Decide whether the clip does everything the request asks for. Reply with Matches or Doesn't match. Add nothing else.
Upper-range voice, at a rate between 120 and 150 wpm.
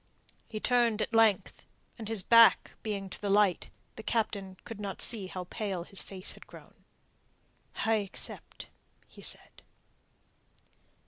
Matches